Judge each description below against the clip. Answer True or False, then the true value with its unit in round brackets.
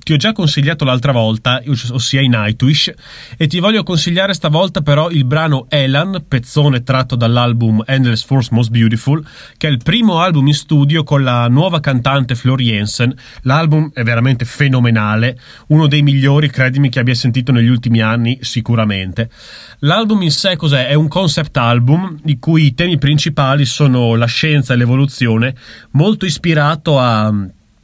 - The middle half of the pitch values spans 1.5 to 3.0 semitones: False (4.1 semitones)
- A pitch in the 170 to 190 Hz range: False (135 Hz)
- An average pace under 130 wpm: False (160 wpm)